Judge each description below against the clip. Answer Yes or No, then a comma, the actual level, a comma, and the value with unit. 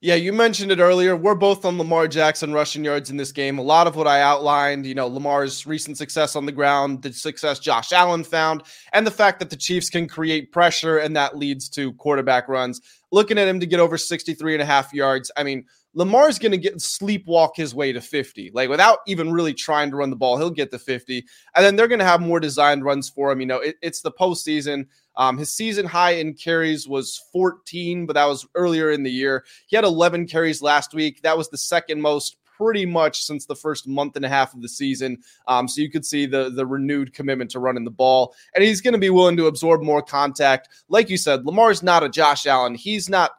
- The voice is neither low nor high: Yes, medium, 155 Hz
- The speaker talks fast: Yes, fast, 240 wpm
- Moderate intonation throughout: Yes, average, 3.7 semitones